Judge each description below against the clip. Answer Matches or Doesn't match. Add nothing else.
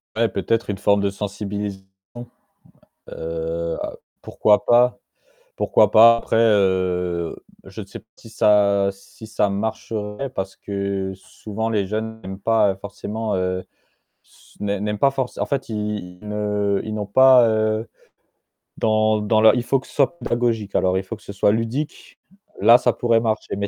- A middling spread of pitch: Doesn't match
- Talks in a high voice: Doesn't match